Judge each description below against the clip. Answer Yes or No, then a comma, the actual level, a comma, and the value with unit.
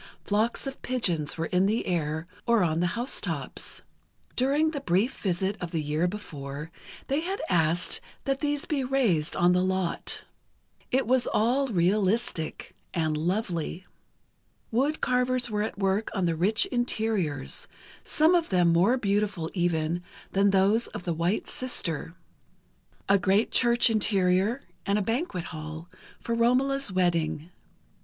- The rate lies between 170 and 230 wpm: No, average, 145 wpm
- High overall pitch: Yes, high, 195 Hz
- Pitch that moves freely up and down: Yes, wide, 5.9 semitones